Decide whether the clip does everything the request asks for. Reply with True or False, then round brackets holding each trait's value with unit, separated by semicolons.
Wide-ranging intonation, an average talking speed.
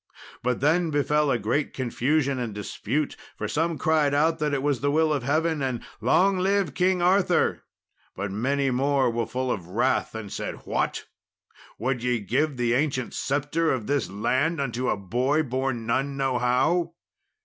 False (4.0 semitones; 170 wpm)